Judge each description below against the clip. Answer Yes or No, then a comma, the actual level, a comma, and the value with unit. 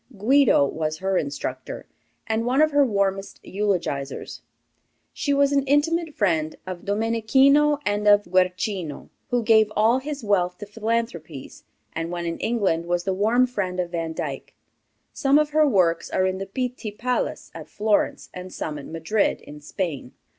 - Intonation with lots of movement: Yes, wide, 5.9 semitones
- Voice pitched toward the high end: Yes, high, 205 Hz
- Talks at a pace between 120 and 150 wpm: No, average, 160 wpm